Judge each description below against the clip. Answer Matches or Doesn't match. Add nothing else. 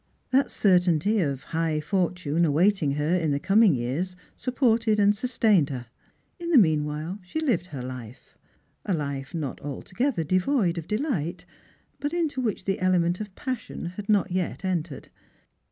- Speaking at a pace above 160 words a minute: Doesn't match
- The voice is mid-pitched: Matches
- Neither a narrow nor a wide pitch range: Doesn't match